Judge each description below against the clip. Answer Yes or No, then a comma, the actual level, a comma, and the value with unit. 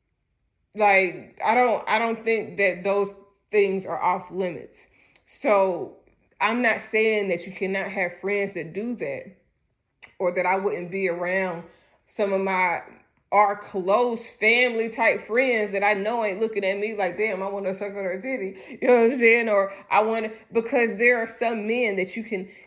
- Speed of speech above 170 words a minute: Yes, average, 185 wpm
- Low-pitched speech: No, high, 200 Hz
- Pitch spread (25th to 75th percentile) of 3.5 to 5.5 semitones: No, average, 2.9 semitones